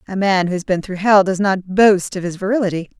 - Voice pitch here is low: No, high, 190 Hz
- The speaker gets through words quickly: Yes, fast, 260 wpm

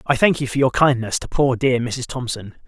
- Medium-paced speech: No, fast, 245 wpm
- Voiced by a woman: No, male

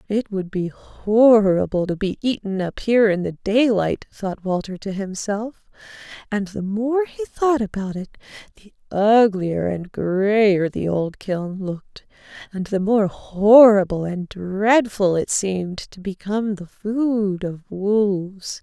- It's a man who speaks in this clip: No, female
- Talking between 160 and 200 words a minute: No, average, 145 wpm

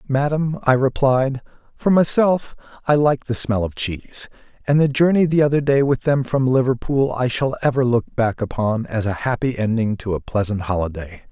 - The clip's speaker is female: No, male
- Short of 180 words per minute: No, average, 185 wpm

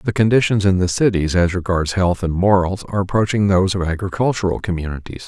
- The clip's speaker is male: Yes, male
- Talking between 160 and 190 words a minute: Yes, average, 180 wpm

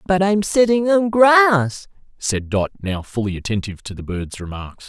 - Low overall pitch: No, medium, 145 Hz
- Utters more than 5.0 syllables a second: No, 4.6 syllables/s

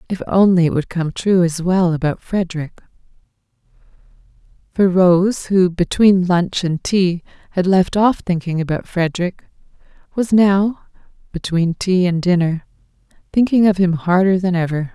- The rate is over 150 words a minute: No, average, 140 wpm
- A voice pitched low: No, medium, 180 Hz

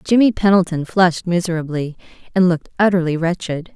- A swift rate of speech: No, slow, 130 wpm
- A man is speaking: No, female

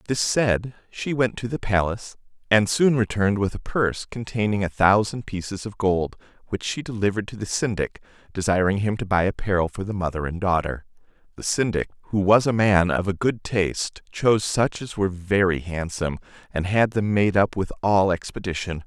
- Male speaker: Yes, male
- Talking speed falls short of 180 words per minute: No, average, 190 wpm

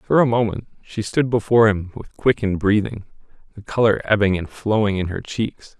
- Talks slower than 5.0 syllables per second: No, 5.3 syllables/s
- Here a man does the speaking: Yes, male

